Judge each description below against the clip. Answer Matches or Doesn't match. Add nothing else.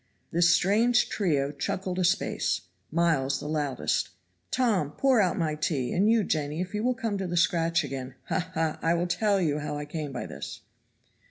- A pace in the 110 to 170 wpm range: Doesn't match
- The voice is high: Doesn't match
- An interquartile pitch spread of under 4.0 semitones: Doesn't match